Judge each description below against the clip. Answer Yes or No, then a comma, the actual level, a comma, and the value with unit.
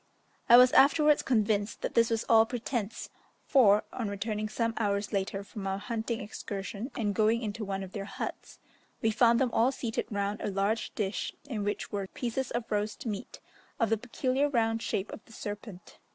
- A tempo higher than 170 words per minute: Yes, average, 185 wpm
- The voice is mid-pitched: No, high, 220 Hz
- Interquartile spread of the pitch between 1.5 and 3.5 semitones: Yes, narrow, 2.5 semitones